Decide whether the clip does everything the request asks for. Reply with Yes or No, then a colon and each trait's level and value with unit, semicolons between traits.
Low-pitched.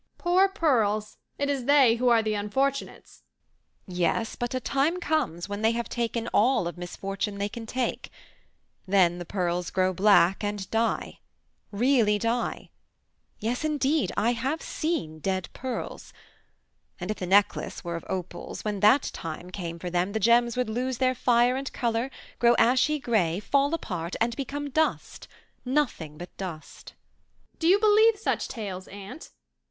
No: high, 230 Hz